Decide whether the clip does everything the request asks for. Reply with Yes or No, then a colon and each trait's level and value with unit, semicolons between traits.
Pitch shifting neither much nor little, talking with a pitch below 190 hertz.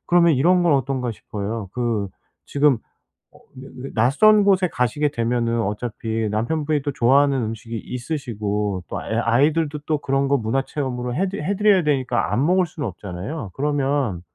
Yes: average, 4.7 semitones; low, 135 Hz